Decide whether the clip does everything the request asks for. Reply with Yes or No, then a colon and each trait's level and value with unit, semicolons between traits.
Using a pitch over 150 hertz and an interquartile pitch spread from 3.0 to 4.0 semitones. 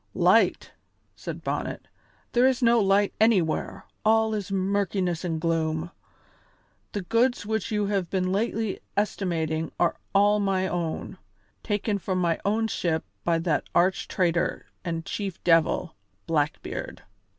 Yes: high, 190 Hz; average, 3.6 semitones